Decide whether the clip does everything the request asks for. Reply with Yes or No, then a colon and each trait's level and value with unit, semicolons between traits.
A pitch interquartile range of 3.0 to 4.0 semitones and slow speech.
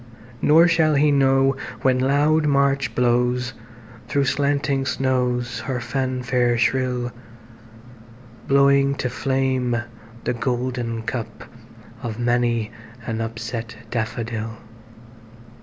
No: narrow, 2.4 semitones; slow, 85 wpm